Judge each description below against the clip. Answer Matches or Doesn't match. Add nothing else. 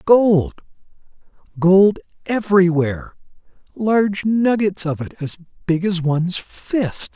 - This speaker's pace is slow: Matches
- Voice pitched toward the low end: Doesn't match